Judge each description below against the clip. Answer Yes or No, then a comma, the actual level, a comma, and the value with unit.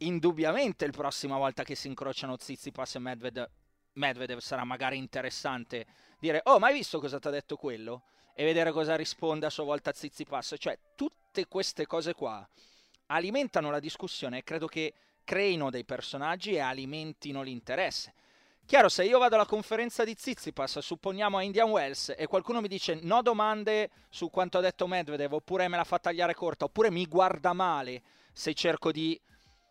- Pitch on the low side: No, medium, 160 Hz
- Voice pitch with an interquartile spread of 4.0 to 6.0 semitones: Yes, wide, 5.5 semitones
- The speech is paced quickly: Yes, fast, 180 wpm